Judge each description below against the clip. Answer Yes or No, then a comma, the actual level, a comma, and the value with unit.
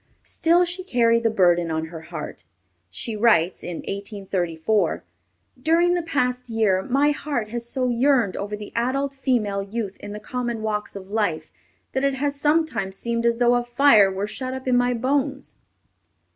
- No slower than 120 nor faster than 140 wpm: No, average, 170 wpm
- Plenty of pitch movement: No, average, 4.9 semitones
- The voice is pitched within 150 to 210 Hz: No, high, 235 Hz